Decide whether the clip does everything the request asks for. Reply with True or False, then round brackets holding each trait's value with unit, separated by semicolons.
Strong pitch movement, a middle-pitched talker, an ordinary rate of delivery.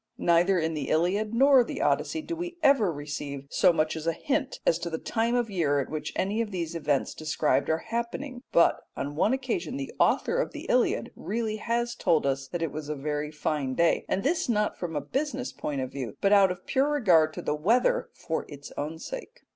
False (7.7 semitones; 175 Hz; 220 wpm)